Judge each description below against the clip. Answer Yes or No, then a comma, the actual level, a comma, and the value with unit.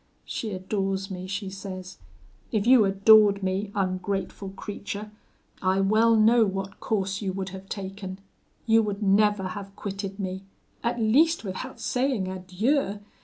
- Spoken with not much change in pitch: Yes, narrow, 2.1 semitones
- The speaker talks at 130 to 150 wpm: Yes, average, 140 wpm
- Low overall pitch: No, high, 195 Hz